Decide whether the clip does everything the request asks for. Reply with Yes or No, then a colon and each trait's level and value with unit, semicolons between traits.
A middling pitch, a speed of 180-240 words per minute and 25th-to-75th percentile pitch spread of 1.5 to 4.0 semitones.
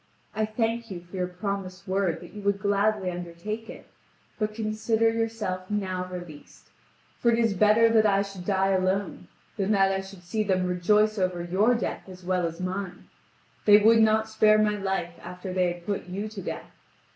No: high, 195 Hz; average, 190 wpm; average, 2.7 semitones